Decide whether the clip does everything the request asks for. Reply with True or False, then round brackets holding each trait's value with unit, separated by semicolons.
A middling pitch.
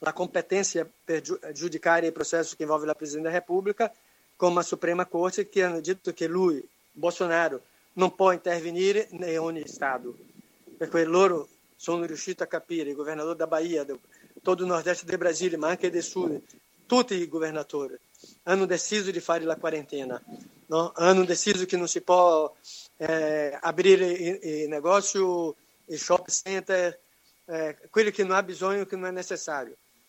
True (175 Hz)